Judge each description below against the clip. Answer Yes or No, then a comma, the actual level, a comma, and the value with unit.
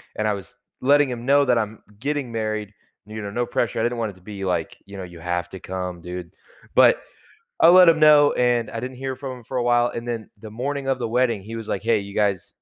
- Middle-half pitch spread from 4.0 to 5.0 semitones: Yes, average, 4.3 semitones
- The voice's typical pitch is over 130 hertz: No, low, 115 Hz